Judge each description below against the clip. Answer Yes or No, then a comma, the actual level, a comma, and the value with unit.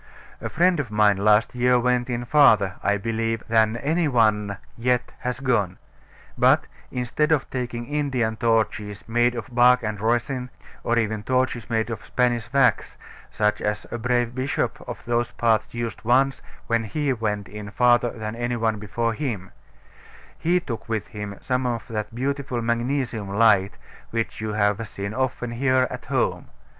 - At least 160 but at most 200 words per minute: Yes, average, 165 wpm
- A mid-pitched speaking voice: No, low, 120 Hz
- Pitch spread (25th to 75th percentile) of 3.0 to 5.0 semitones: No, narrow, 2.6 semitones